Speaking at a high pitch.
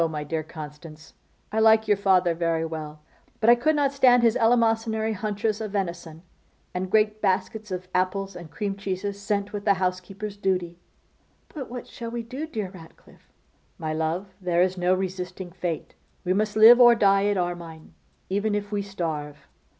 Yes: high, 195 Hz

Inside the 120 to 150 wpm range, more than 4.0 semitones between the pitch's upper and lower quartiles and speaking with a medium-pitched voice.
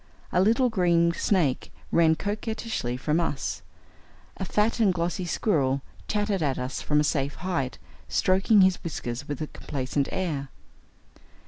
Yes: average, 140 wpm; wide, 5.5 semitones; medium, 170 Hz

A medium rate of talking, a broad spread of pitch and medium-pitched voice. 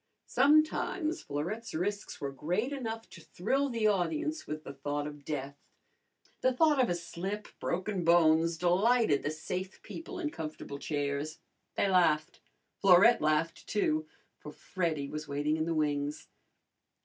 Yes: average, 145 wpm; wide, 6.6 semitones; medium, 170 Hz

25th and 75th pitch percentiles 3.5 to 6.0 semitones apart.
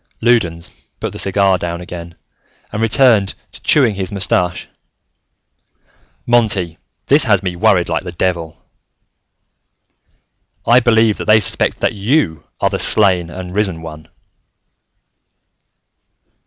Yes: average, 4.2 semitones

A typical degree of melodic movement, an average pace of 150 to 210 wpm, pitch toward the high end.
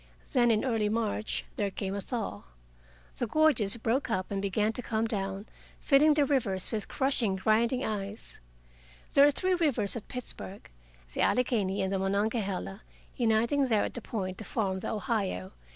Yes: average, 4.0 semitones; average, 170 wpm; high, 220 Hz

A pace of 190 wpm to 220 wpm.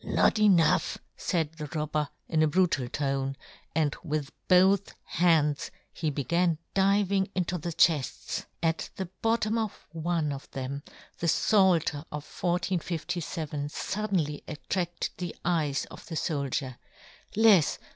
No: slow, 135 wpm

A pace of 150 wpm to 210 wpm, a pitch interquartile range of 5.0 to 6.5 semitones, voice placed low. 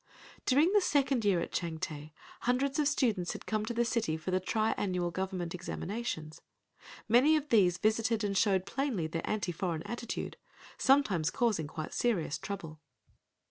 No: average, 155 wpm; wide, 5.6 semitones; high, 205 Hz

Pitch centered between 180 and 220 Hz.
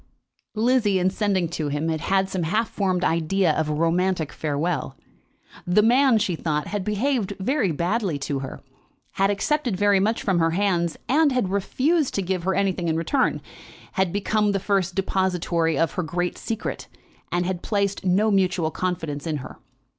Yes: high, 190 Hz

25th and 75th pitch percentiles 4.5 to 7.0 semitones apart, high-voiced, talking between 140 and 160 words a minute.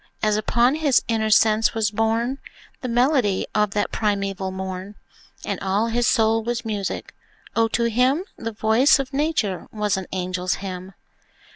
No: average, 3.3 semitones; high, 220 Hz; average, 155 wpm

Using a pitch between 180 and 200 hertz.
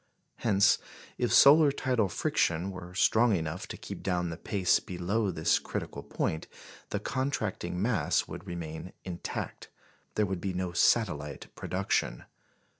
No: very low, 90 Hz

